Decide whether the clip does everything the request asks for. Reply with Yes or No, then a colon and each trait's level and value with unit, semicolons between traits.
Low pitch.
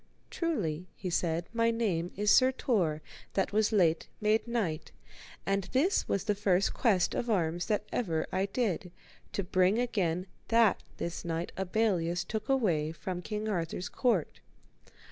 No: high, 195 Hz